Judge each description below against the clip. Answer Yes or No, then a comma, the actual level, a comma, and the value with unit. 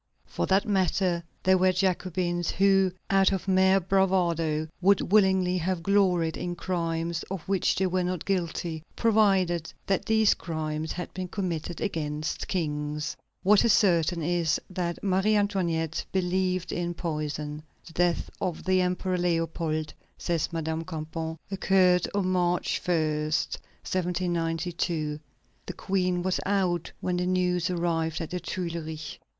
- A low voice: No, medium, 180 Hz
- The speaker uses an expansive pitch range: No, narrow, 2.4 semitones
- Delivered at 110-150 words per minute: Yes, slow, 135 wpm